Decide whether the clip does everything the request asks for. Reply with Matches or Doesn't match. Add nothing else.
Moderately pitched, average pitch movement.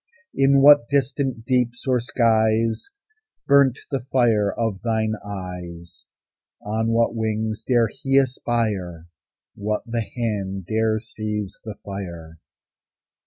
Doesn't match